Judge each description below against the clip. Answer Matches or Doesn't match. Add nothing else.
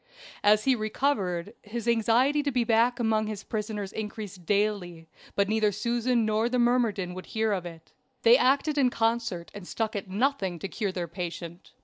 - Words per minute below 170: Doesn't match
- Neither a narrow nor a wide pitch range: Matches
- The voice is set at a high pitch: Matches